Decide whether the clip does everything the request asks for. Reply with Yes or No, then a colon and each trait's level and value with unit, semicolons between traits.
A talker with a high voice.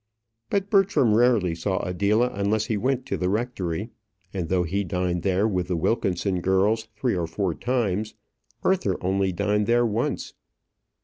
No: low, 100 Hz